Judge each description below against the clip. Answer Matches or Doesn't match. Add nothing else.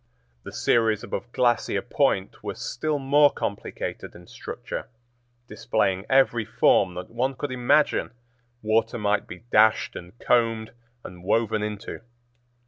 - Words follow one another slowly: Matches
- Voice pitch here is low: Matches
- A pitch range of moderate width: Matches